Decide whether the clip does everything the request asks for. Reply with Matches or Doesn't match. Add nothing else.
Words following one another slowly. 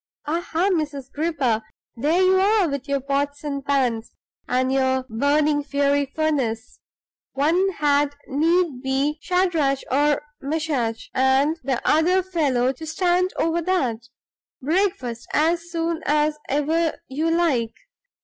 Matches